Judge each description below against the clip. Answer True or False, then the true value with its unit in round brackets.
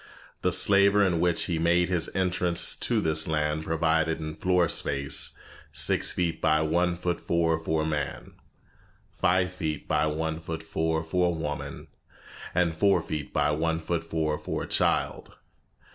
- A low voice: True (80 Hz)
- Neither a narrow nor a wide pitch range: False (1.9 semitones)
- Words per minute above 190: False (160 wpm)